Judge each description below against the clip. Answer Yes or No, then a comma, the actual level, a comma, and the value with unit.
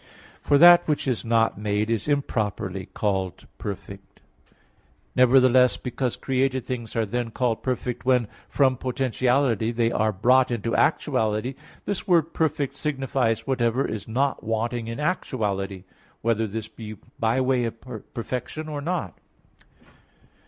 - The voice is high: No, low, 120 Hz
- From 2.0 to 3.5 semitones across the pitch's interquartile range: Yes, average, 3.2 semitones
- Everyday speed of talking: No, slow, 130 wpm